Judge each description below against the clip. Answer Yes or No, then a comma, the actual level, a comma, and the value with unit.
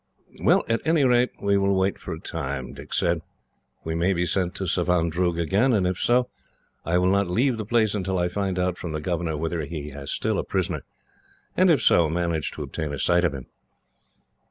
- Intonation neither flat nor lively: Yes, average, 3.2 semitones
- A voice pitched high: No, very low, 90 Hz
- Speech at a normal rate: No, fast, 210 wpm